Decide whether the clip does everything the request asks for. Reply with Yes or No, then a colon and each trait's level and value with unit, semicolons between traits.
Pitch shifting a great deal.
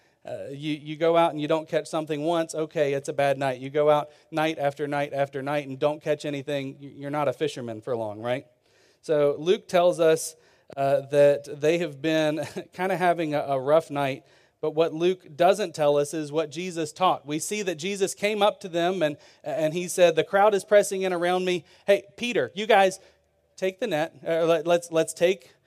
No: average, 3.5 semitones